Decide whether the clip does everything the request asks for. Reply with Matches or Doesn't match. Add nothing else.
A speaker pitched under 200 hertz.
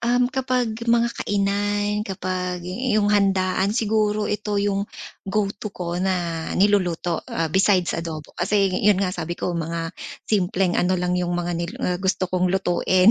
Matches